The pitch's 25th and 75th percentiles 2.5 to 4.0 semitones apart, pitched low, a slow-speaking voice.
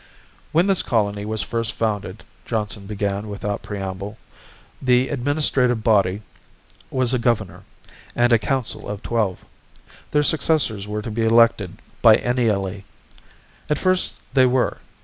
Yes: average, 3.5 semitones; low, 110 Hz; slow, 130 wpm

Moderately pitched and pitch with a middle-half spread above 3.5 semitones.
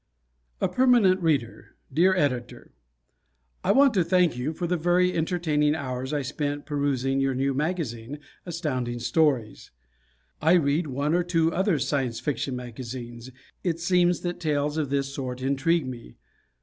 Yes: medium, 150 Hz; average, 4.8 semitones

